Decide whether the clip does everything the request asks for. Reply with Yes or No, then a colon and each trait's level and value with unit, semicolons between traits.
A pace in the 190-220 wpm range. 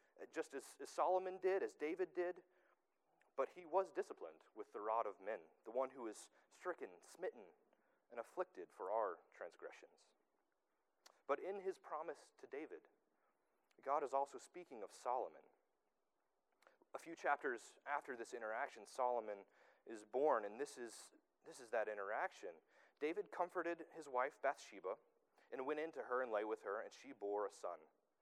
No: average, 155 wpm